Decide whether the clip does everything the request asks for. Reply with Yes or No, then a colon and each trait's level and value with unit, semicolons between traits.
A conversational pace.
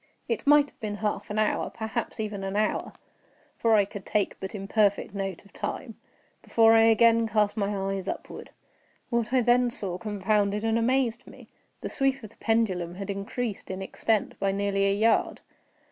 Yes: average, 180 wpm